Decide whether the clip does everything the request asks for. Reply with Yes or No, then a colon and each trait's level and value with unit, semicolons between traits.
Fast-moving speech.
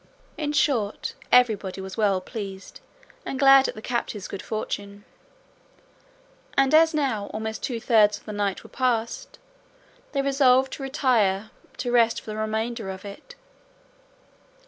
No: average, 145 wpm